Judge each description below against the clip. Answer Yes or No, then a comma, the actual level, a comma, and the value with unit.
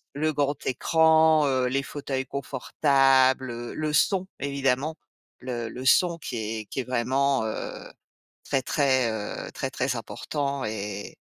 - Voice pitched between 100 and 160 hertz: Yes, low, 135 Hz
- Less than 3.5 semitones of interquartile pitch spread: Yes, narrow, 2.5 semitones